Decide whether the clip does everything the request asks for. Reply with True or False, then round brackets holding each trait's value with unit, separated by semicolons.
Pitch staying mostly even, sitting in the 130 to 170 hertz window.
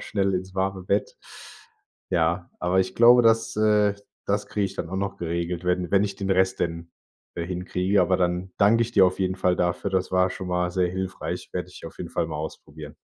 False (1.8 semitones; 95 Hz)